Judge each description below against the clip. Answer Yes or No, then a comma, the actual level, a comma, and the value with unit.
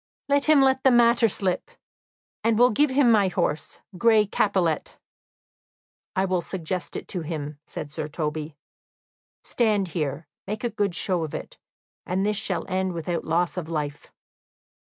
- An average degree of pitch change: No, wide, 5.7 semitones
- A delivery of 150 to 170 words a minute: Yes, average, 155 wpm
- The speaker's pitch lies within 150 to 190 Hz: Yes, medium, 185 Hz